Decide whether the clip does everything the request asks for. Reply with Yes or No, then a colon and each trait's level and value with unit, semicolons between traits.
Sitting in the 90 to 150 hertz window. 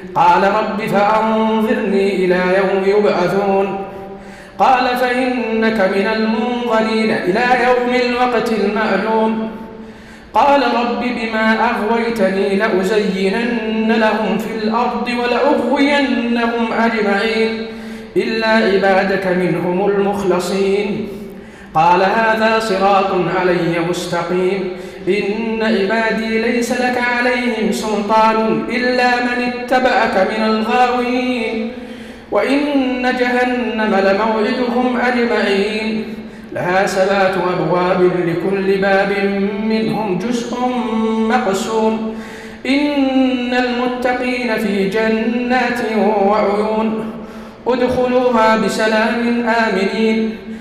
No: high, 220 Hz